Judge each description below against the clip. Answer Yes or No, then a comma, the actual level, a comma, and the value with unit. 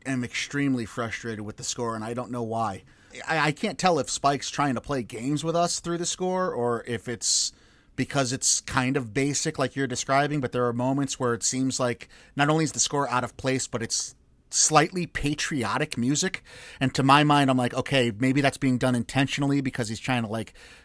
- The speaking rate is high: Yes, fast, 215 wpm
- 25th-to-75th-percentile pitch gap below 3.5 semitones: Yes, average, 3.0 semitones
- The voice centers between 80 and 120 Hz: No, low, 130 Hz